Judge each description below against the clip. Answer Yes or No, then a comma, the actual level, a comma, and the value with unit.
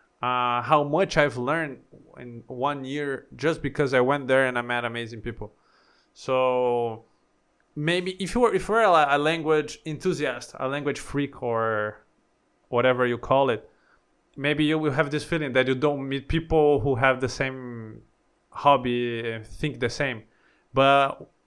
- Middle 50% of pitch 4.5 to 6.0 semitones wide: No, average, 3.6 semitones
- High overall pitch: No, low, 135 Hz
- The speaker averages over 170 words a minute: No, average, 155 wpm